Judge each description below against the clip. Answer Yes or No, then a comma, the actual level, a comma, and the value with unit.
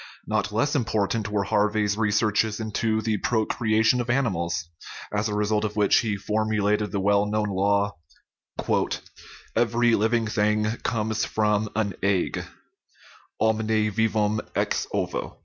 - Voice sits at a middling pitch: No, low, 105 Hz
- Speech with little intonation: Yes, narrow, 1.2 semitones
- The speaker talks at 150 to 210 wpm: No, average, 140 wpm